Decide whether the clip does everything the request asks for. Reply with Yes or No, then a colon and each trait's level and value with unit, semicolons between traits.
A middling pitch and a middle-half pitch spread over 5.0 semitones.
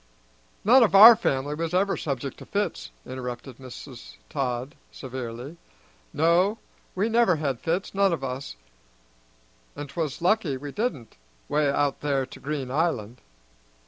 Yes: medium, 145 Hz; wide, 5.5 semitones